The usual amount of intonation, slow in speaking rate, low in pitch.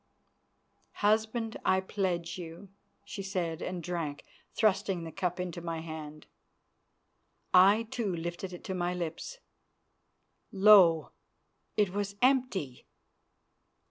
No: average, 3.3 semitones; slow, 110 wpm; medium, 185 Hz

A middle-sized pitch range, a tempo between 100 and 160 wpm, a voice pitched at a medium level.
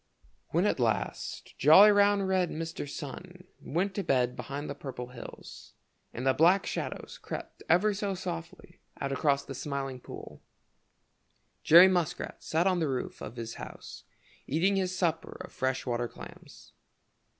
No: wide, 5.9 semitones; average, 150 wpm; medium, 160 Hz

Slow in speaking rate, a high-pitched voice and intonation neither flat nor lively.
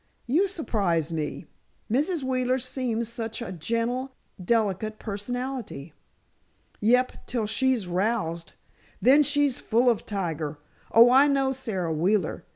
Yes: slow, 120 wpm; high, 230 Hz; average, 5.0 semitones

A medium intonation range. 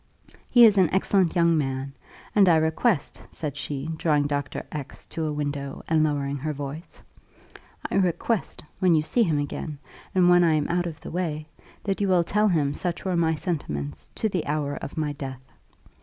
Yes: average, 3.6 semitones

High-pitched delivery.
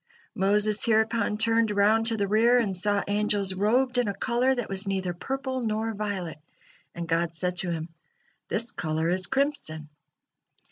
Yes: high, 210 Hz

